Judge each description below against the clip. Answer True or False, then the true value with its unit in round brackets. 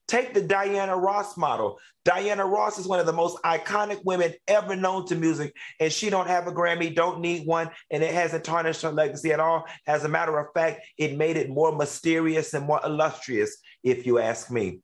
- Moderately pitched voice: True (165 Hz)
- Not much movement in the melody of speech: False (3.5 semitones)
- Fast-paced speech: True (210 wpm)